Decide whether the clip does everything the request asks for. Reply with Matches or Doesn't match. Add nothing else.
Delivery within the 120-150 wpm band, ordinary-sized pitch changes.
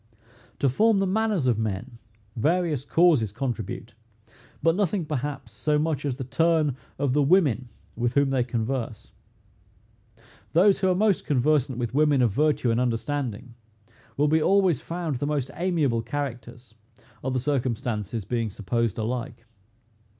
Matches